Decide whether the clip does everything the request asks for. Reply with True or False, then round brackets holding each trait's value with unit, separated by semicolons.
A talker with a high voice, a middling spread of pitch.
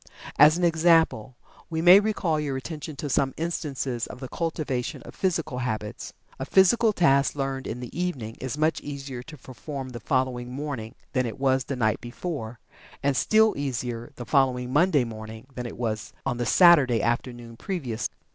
False (135 Hz; 4.6 semitones)